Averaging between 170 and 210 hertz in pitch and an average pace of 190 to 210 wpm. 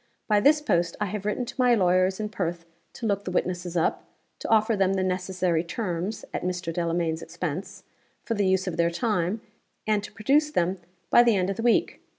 Yes: high, 190 Hz; fast, 205 wpm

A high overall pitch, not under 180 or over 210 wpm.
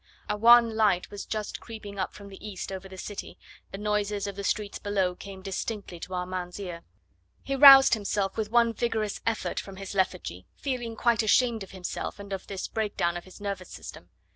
Yes: high, 200 Hz; average, 195 wpm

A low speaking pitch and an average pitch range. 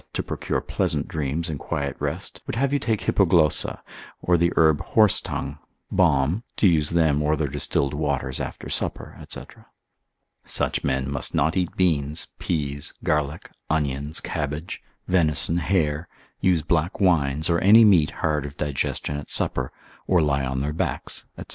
Yes: very low, 75 Hz; average, 3.3 semitones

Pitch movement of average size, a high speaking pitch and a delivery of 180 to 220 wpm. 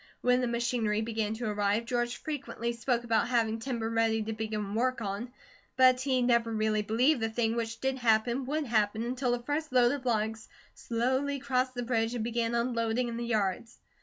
No: narrow, 2.1 semitones; high, 235 Hz; average, 190 wpm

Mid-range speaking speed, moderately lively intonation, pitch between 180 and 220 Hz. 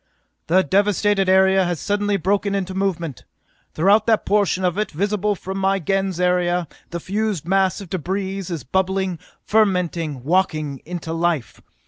No: average, 145 wpm; narrow, 2.3 semitones; high, 190 Hz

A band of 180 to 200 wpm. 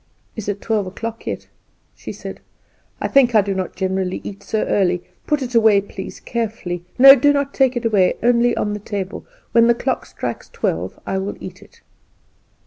Yes: average, 190 wpm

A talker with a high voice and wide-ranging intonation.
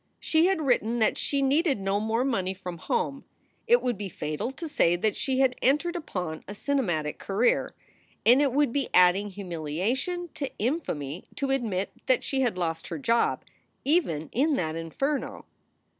Yes: high, 235 Hz; wide, 7.3 semitones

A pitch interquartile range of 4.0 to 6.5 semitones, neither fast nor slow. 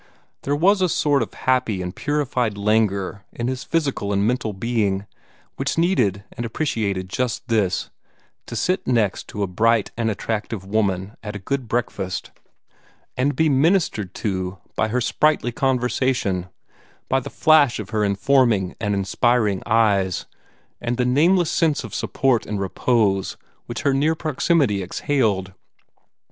Yes: average, 5.2 semitones; average, 145 wpm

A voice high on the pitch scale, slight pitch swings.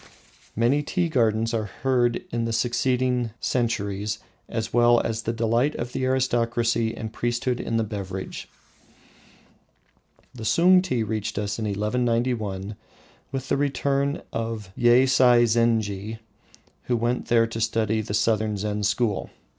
No: low, 115 Hz; narrow, 2.2 semitones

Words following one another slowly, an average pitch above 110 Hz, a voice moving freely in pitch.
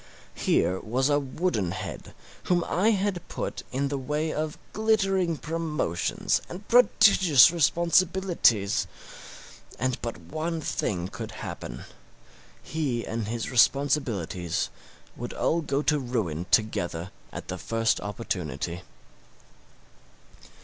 Yes: slow, 110 wpm; medium, 140 Hz; wide, 7.9 semitones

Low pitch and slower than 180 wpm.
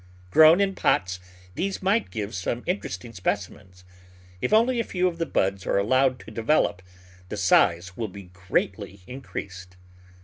Yes: low, 110 Hz; average, 160 wpm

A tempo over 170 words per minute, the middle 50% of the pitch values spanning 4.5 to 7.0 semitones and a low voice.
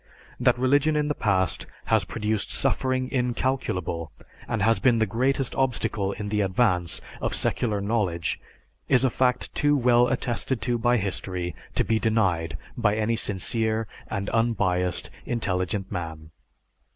No: average, 140 wpm; average, 4.8 semitones; low, 110 Hz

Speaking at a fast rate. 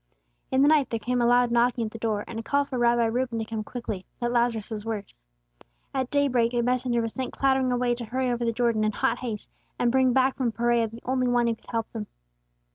Yes: fast, 250 wpm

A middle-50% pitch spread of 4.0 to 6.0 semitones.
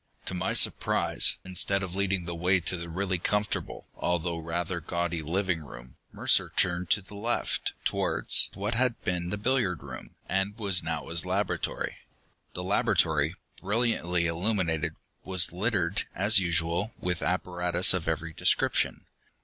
No: average, 2.7 semitones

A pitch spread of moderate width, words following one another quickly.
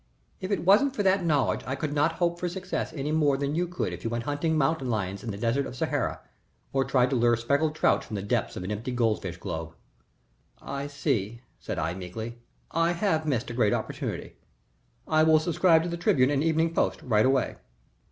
No: wide, 5.7 semitones; fast, 210 wpm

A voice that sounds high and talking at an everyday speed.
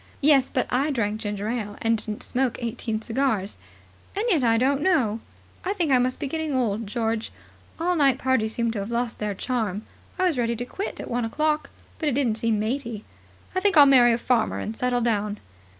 No: high, 240 Hz; fast, 210 wpm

